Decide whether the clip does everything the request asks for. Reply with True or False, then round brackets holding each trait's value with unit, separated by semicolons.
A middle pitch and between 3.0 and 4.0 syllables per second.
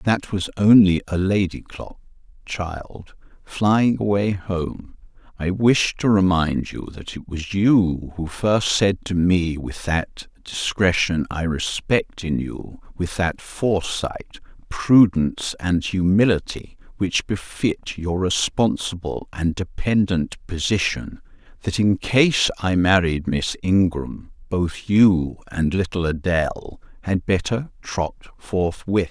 False (90 Hz; 3.5 syllables/s)